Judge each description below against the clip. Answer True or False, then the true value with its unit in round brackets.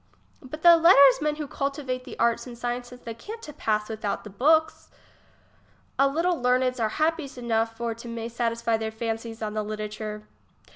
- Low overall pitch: False (240 Hz)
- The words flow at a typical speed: True (155 wpm)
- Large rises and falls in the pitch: False (3.8 semitones)